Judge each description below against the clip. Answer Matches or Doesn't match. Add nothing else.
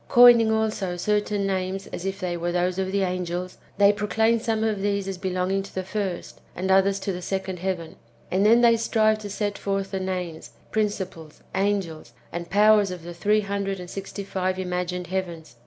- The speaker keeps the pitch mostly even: Matches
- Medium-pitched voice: Doesn't match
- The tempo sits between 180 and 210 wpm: Matches